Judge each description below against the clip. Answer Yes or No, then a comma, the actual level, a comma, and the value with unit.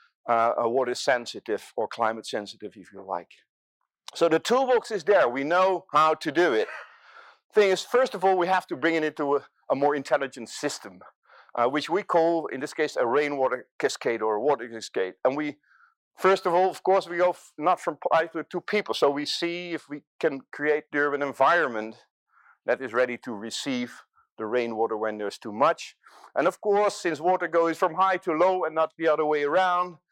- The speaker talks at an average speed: No, fast, 210 wpm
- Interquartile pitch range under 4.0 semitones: No, wide, 5.6 semitones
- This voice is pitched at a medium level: Yes, medium, 160 Hz